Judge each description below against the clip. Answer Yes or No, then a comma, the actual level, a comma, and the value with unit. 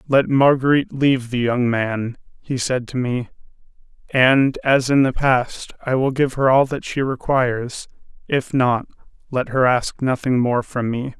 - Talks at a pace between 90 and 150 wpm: No, average, 170 wpm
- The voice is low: Yes, low, 130 Hz